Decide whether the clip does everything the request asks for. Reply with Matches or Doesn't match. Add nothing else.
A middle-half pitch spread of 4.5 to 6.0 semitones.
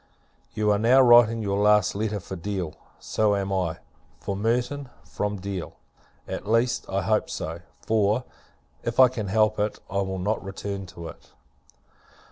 Doesn't match